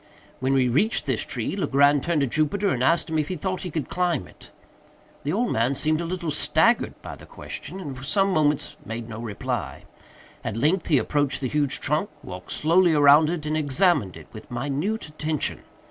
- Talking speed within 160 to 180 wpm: No, average, 200 wpm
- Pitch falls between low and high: Yes, medium, 150 Hz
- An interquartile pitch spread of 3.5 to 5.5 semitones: Yes, average, 4.2 semitones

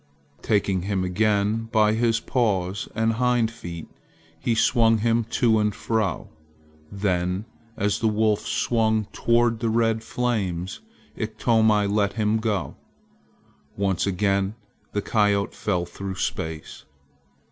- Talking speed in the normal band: No, slow, 120 wpm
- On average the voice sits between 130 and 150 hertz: No, low, 105 Hz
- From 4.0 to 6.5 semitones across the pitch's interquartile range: No, narrow, 2.5 semitones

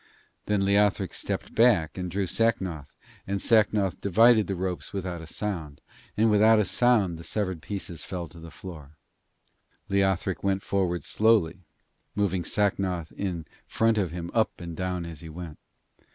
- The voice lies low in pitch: Yes, very low, 95 Hz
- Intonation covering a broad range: No, average, 3.3 semitones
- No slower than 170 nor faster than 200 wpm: No, average, 155 wpm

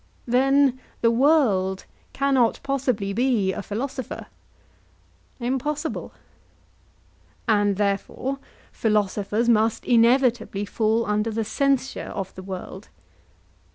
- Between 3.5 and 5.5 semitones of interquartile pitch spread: Yes, average, 4.3 semitones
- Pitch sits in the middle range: No, high, 230 Hz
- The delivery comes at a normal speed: No, slow, 90 wpm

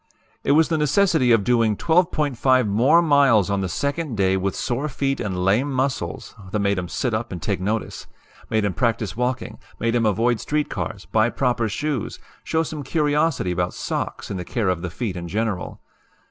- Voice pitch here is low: Yes, low, 115 Hz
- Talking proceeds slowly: No, average, 190 wpm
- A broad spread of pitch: Yes, wide, 6.0 semitones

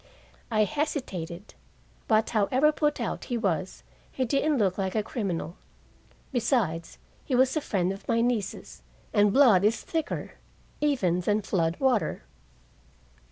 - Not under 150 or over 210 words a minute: No, slow, 135 wpm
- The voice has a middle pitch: No, high, 215 Hz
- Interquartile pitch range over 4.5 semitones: Yes, wide, 5.6 semitones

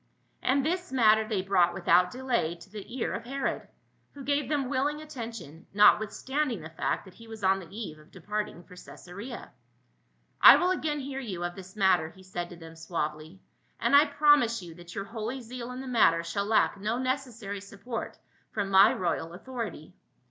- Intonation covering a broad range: Yes, wide, 6.3 semitones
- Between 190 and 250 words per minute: Yes, average, 200 wpm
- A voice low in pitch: No, high, 215 Hz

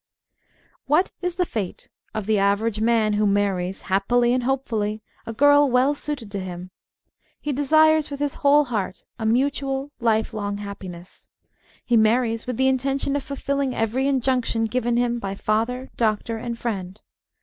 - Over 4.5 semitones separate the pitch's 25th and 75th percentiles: No, average, 4.2 semitones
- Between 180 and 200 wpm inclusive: No, average, 160 wpm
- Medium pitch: No, high, 235 Hz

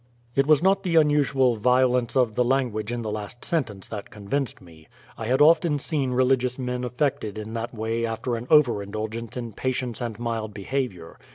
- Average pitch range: Yes, average, 3.5 semitones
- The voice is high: No, low, 120 Hz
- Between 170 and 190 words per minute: Yes, average, 185 wpm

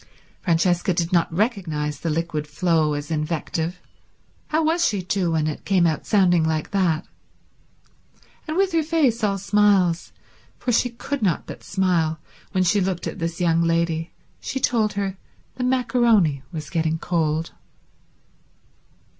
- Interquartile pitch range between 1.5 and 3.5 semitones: No, average, 4.3 semitones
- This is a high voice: No, medium, 175 Hz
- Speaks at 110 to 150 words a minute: Yes, average, 145 wpm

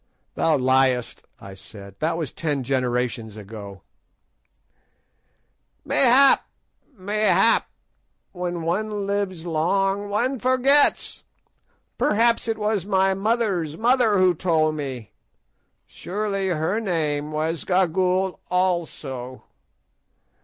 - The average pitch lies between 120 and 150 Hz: No, medium, 180 Hz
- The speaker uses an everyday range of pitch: No, wide, 5.9 semitones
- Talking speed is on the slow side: Yes, slow, 95 wpm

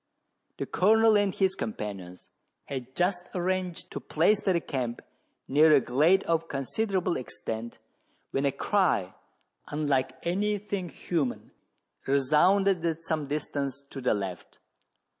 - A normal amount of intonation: No, wide, 5.8 semitones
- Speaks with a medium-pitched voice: Yes, medium, 155 Hz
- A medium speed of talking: No, slow, 125 wpm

